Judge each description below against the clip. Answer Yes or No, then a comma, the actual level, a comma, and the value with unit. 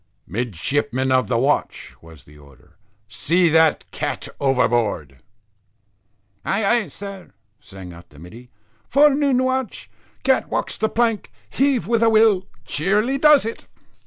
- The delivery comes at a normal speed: No, slow, 130 wpm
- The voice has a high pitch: No, medium, 160 Hz